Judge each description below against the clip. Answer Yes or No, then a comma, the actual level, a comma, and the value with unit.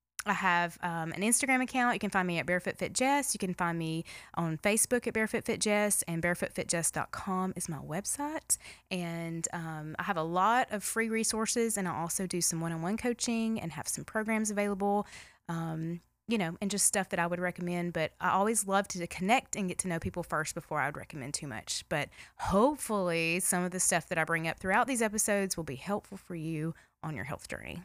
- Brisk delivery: Yes, fast, 220 wpm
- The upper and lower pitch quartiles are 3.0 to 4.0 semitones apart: No, average, 4.4 semitones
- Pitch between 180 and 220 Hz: Yes, medium, 185 Hz